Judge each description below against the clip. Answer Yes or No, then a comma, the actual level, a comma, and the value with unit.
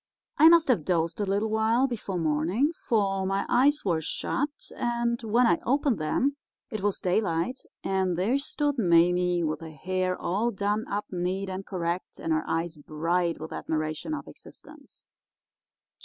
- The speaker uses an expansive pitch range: Yes, wide, 5.7 semitones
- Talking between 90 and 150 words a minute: No, average, 160 wpm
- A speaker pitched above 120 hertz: Yes, high, 190 Hz